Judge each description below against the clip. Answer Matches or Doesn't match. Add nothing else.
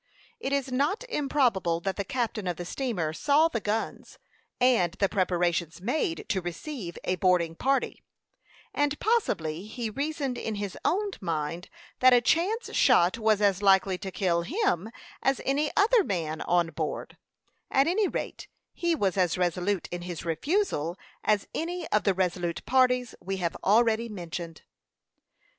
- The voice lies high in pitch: Matches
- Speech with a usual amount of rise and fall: Doesn't match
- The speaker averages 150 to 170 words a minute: Matches